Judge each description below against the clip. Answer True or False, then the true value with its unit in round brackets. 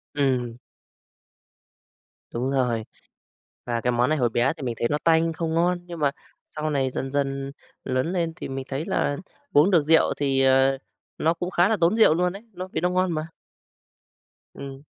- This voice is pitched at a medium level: True (145 Hz)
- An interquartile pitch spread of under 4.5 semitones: True (4.0 semitones)